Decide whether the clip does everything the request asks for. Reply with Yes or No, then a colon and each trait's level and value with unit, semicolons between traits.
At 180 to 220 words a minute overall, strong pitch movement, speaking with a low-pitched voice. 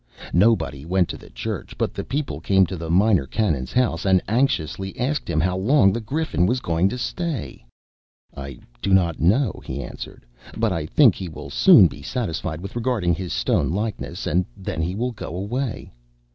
Yes: average, 185 wpm; wide, 6.1 semitones; very low, 95 Hz